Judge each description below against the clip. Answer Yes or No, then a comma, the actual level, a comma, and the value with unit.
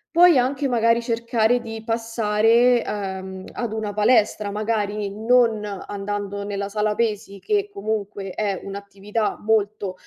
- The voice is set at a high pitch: Yes, high, 215 Hz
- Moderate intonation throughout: No, narrow, 2.3 semitones